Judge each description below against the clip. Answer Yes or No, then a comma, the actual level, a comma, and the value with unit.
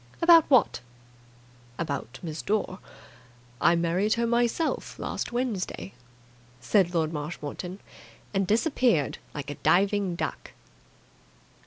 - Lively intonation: Yes, wide, 5.9 semitones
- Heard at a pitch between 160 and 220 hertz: Yes, high, 190 Hz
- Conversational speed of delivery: No, slow, 105 wpm